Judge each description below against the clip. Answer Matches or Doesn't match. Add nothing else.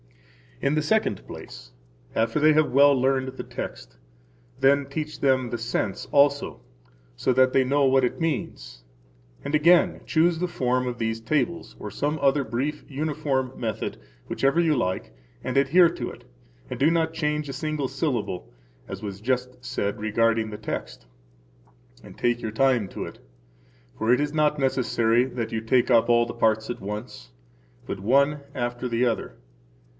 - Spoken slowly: Doesn't match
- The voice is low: Matches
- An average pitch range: Matches